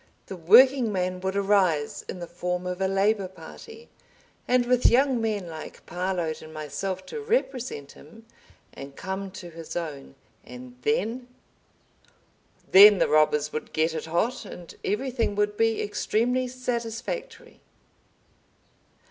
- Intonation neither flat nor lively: No, wide, 6.0 semitones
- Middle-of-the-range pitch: No, high, 195 Hz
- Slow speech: Yes, slow, 130 wpm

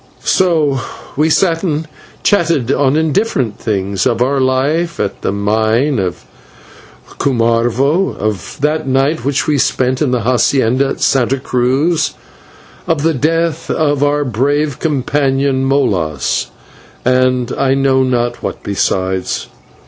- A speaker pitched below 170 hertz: Yes, low, 135 Hz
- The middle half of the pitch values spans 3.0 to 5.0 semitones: Yes, average, 3.7 semitones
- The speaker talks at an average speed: No, slow, 125 wpm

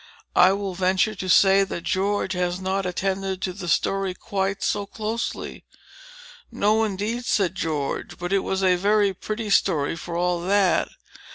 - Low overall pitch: No, high, 190 Hz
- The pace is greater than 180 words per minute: No, average, 160 wpm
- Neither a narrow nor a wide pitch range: No, narrow, 1.9 semitones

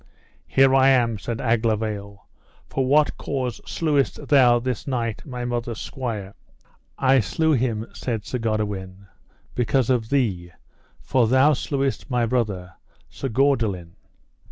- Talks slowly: Yes, slow, 130 wpm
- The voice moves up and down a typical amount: Yes, average, 3.6 semitones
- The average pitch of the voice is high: No, low, 120 Hz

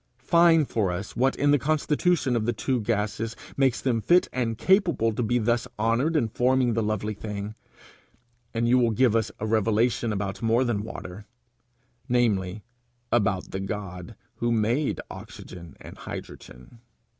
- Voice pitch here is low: Yes, low, 115 Hz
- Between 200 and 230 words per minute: No, average, 155 wpm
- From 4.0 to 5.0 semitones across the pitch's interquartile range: No, average, 3.3 semitones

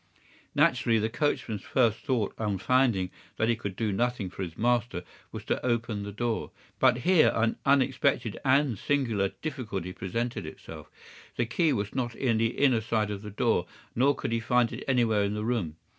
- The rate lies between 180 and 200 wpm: Yes, average, 185 wpm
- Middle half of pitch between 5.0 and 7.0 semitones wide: No, average, 3.4 semitones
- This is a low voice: Yes, low, 115 Hz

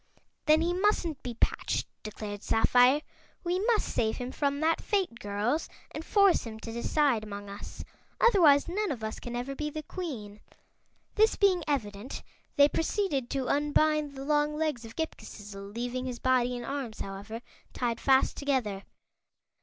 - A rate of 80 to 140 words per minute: No, average, 160 wpm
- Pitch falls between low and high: No, very high, 270 Hz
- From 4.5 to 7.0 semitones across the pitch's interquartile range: Yes, wide, 5.4 semitones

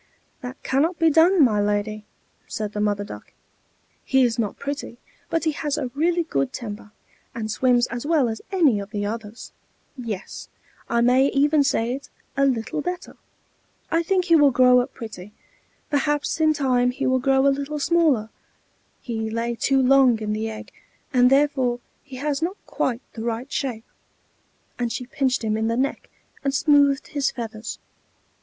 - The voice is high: Yes, very high, 255 Hz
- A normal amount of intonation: Yes, average, 4.2 semitones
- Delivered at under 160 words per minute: No, average, 175 wpm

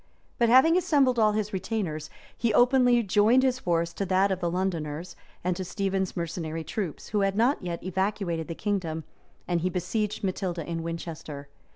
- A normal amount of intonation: Yes, average, 4.3 semitones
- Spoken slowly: No, average, 175 wpm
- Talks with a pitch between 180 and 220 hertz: Yes, high, 190 Hz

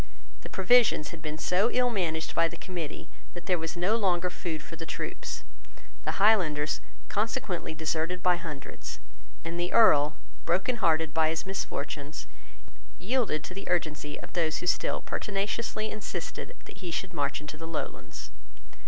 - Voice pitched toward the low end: No, medium, 175 Hz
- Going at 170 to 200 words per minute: No, average, 155 wpm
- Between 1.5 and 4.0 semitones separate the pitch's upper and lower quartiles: Yes, average, 3.5 semitones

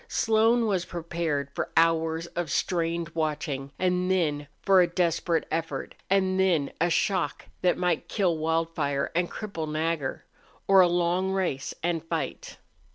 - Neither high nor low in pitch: Yes, medium, 170 Hz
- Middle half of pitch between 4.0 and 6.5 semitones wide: No, narrow, 2.4 semitones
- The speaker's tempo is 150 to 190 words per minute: No, average, 140 wpm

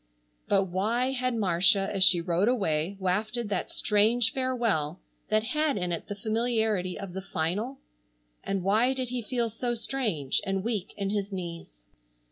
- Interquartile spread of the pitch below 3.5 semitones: No, average, 4.4 semitones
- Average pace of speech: Yes, average, 160 wpm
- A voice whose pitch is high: Yes, high, 205 Hz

